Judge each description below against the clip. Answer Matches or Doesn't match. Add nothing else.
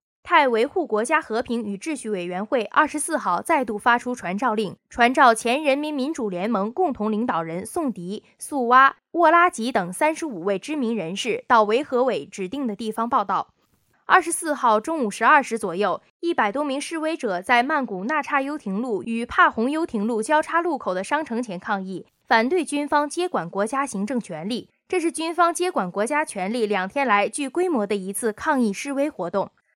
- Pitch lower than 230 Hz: Doesn't match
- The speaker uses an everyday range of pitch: Doesn't match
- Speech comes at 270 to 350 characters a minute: Matches